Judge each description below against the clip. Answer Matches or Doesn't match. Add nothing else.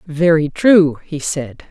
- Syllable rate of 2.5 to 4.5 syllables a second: Matches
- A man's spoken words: Doesn't match